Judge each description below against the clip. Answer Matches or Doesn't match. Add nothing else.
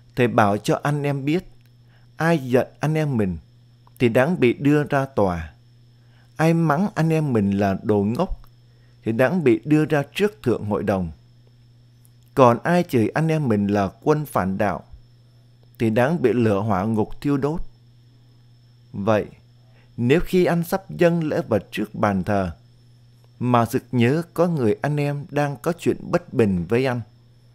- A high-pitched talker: Doesn't match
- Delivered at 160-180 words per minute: Matches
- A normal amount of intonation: Matches